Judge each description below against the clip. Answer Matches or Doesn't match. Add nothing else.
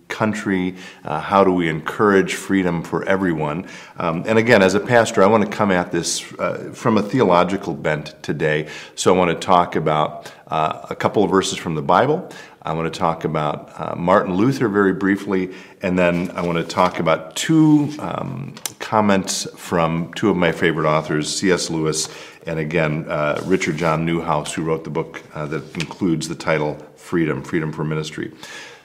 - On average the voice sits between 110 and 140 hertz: Doesn't match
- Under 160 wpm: Doesn't match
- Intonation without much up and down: Doesn't match